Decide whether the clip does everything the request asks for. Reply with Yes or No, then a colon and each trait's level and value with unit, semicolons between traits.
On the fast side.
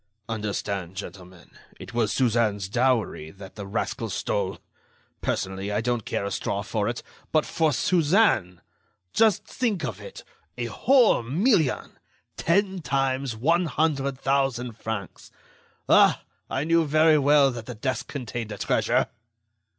No: slow, 135 wpm